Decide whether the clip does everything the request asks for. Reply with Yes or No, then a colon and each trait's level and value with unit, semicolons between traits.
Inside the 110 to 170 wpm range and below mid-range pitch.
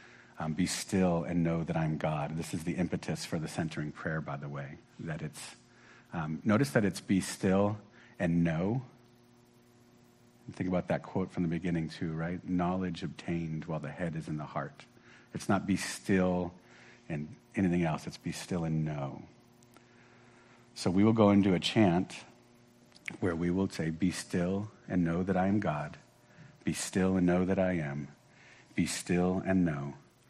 No: average, 180 wpm; very low, 90 Hz